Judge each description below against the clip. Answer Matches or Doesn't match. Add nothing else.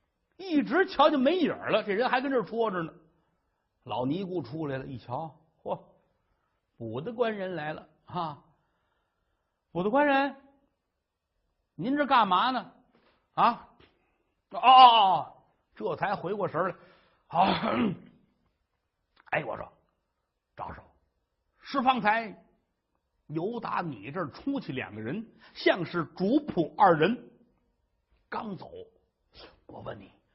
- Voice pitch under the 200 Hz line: Doesn't match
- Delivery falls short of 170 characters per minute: Matches